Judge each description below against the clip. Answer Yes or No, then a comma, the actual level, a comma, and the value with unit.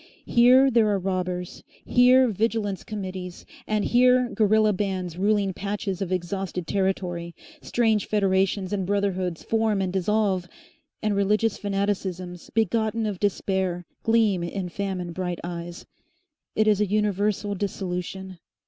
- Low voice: No, high, 195 Hz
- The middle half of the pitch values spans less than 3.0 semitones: Yes, narrow, 2.6 semitones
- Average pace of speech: No, slow, 125 wpm